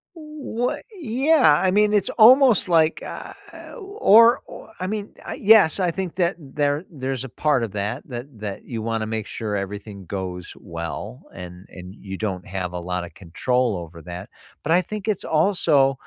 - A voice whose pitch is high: No, low, 135 Hz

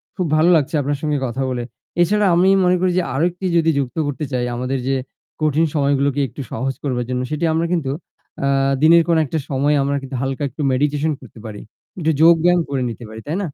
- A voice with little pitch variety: No, average, 3.6 semitones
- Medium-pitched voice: Yes, medium, 145 Hz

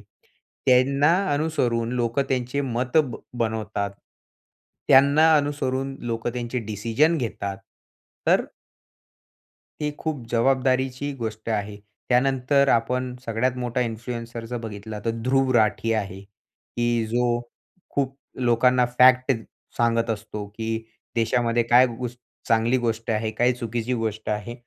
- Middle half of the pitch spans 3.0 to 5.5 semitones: No, narrow, 2.4 semitones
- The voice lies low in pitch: Yes, low, 120 Hz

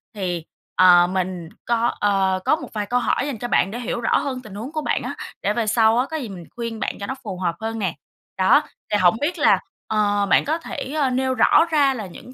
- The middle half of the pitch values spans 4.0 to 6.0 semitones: Yes, average, 5.2 semitones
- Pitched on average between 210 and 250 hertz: Yes, high, 220 Hz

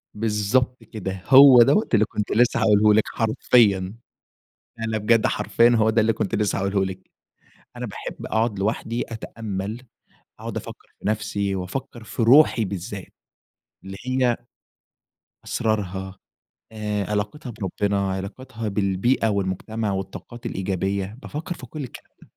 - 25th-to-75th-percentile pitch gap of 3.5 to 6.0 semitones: No, average, 3.0 semitones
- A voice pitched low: Yes, low, 105 Hz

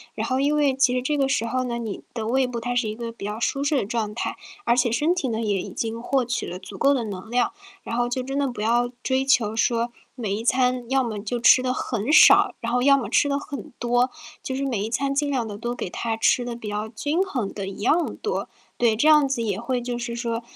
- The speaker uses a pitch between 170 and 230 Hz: No, high, 240 Hz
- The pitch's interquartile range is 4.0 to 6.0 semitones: No, average, 2.9 semitones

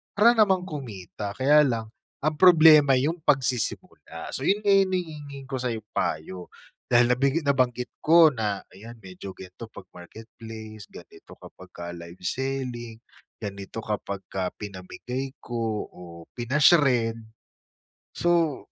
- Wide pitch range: Yes, wide, 6.1 semitones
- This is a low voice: Yes, low, 125 Hz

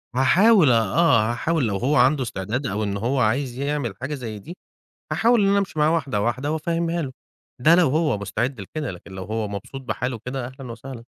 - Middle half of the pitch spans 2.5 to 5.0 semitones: No, wide, 5.5 semitones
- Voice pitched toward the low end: Yes, low, 130 Hz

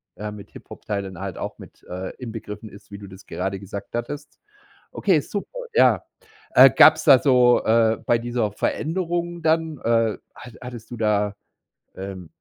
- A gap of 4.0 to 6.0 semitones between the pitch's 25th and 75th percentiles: Yes, average, 4.8 semitones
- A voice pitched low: Yes, low, 115 Hz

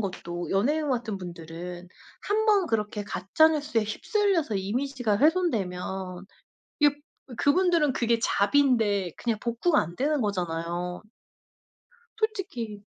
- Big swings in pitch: Yes, wide, 7.8 semitones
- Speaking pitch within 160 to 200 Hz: No, high, 225 Hz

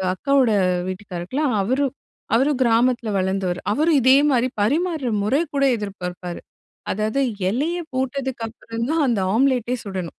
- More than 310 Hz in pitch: No, high, 240 Hz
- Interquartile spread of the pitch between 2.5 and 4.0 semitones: No, average, 5.3 semitones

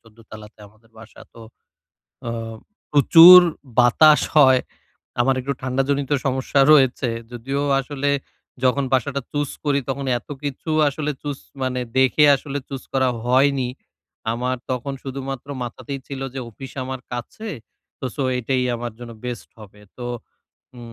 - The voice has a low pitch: Yes, low, 130 Hz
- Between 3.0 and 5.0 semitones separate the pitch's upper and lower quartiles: No, narrow, 2.5 semitones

